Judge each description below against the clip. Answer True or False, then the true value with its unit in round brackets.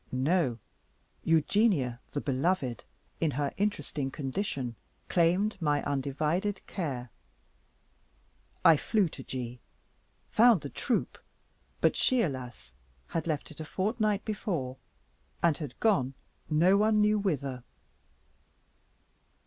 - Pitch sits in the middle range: True (155 Hz)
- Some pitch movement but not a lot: False (7.0 semitones)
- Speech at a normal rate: False (110 wpm)